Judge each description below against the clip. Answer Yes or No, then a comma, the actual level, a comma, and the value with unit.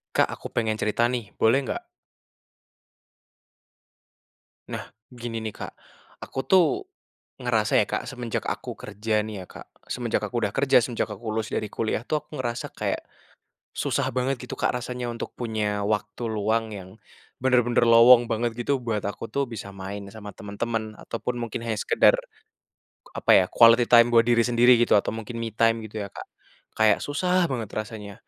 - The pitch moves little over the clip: Yes, narrow, 2.2 semitones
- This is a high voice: No, low, 115 Hz